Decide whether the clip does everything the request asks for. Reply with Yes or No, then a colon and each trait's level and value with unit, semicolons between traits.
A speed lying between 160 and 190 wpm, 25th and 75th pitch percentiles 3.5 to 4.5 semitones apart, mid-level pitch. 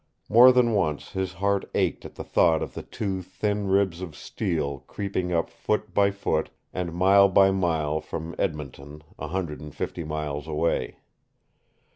No: average, 165 wpm; average, 4.2 semitones; very low, 90 Hz